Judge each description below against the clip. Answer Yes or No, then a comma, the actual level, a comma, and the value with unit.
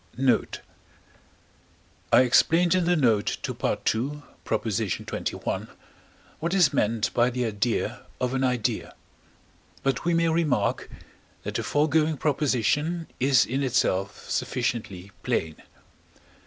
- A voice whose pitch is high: No, low, 130 Hz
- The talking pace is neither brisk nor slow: No, slow, 115 wpm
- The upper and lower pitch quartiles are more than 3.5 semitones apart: Yes, average, 5.2 semitones